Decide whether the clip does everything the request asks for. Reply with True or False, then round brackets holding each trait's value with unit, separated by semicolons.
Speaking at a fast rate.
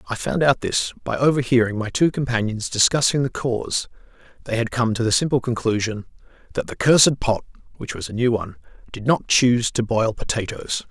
False (185 wpm)